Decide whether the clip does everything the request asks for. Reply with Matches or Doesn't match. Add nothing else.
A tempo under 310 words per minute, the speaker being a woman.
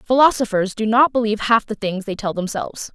Matches